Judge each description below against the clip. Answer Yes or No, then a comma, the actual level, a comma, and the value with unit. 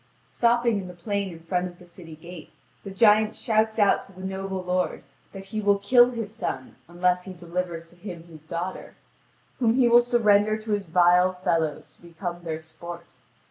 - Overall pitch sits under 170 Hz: No, medium, 185 Hz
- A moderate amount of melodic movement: Yes, average, 3.6 semitones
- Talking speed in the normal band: Yes, average, 190 wpm